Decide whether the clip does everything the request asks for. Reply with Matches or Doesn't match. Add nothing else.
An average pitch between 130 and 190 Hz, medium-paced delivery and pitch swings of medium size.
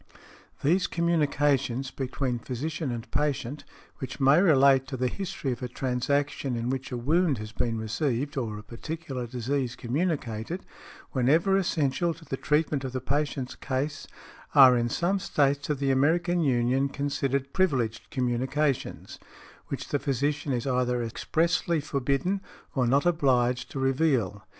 Matches